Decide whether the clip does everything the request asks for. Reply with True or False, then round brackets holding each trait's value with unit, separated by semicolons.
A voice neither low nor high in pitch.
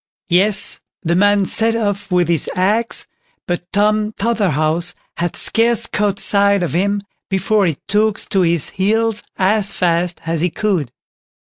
False (200 Hz)